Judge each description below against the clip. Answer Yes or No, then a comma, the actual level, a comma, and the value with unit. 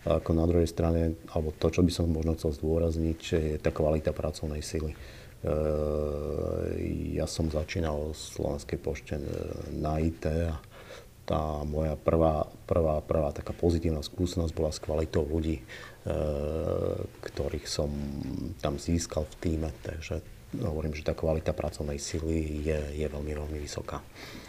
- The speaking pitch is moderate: No, very low, 80 Hz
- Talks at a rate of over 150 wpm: No, average, 140 wpm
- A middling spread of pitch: No, narrow, 1.6 semitones